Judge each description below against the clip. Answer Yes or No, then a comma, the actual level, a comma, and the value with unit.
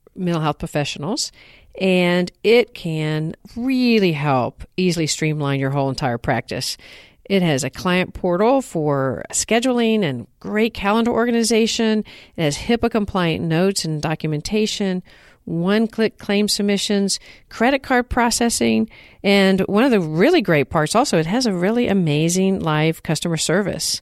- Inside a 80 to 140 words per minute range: Yes, slow, 135 wpm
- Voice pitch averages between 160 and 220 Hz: Yes, medium, 185 Hz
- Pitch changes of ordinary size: No, wide, 6.0 semitones